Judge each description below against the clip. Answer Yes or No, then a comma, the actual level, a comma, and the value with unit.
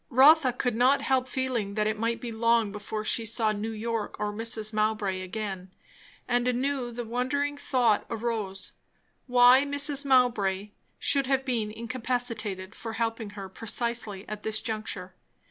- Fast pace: No, average, 150 wpm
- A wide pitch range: No, average, 3.0 semitones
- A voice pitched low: No, high, 230 Hz